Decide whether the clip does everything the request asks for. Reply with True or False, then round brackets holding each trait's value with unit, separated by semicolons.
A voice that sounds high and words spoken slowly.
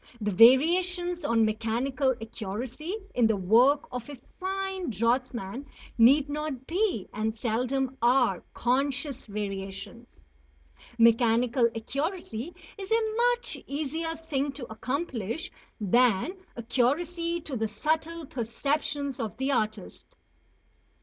True (260 Hz; 110 wpm)